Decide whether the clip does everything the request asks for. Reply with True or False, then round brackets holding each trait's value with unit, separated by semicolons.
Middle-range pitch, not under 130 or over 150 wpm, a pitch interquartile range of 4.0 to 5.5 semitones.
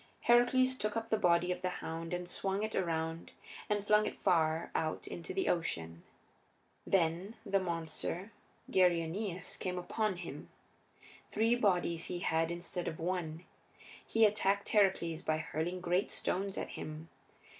False (180 Hz; 145 wpm; 3.4 semitones)